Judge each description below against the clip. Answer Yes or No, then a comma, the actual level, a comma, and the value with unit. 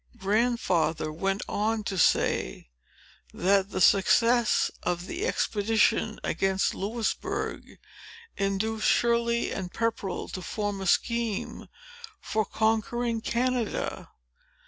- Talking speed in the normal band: No, slow, 100 wpm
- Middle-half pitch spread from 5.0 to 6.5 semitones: No, average, 3.3 semitones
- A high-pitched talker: Yes, high, 215 Hz